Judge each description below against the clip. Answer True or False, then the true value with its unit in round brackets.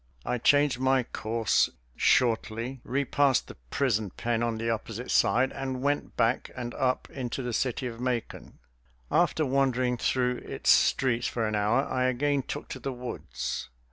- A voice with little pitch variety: True (2.2 semitones)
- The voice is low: True (125 Hz)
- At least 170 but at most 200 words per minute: False (160 wpm)